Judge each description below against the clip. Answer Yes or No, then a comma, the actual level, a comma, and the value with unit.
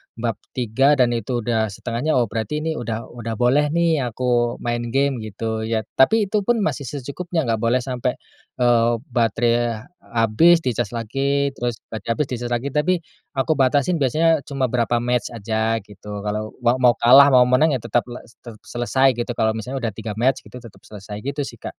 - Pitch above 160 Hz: No, low, 120 Hz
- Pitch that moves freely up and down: No, average, 3.2 semitones